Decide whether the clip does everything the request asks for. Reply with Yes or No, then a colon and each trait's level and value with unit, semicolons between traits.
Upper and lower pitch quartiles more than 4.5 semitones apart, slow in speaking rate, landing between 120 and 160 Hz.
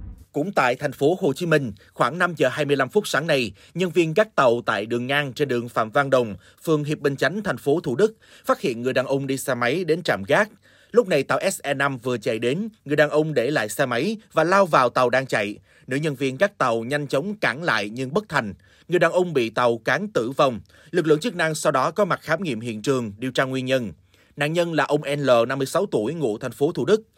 No: average, 5.1 semitones; fast, 250 wpm; medium, 140 Hz